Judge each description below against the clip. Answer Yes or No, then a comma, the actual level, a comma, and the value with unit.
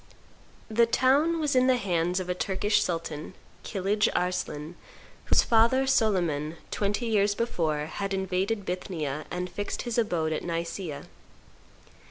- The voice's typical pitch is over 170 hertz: Yes, high, 190 Hz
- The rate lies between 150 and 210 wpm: No, slow, 135 wpm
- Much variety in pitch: No, average, 5.0 semitones